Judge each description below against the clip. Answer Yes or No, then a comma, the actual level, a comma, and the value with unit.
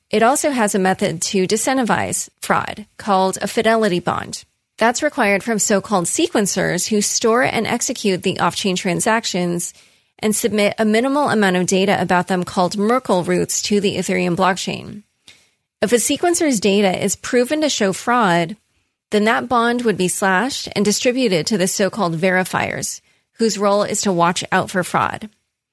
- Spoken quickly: No, average, 160 wpm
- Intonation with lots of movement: No, average, 3.4 semitones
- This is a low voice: No, high, 205 Hz